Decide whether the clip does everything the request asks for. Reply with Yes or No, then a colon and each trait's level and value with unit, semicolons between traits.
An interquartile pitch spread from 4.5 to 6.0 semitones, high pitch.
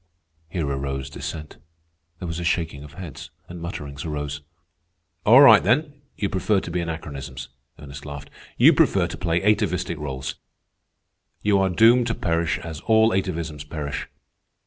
No: average, 4.8 semitones; very low, 85 Hz